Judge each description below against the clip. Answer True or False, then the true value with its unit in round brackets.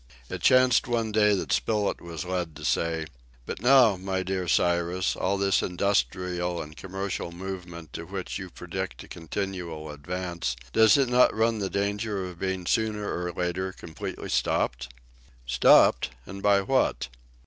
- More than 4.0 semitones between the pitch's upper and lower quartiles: False (2.9 semitones)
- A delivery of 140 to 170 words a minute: True (155 wpm)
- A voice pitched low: True (95 Hz)